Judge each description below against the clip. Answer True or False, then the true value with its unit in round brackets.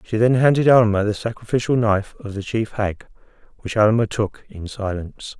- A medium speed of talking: True (180 wpm)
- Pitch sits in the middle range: False (110 Hz)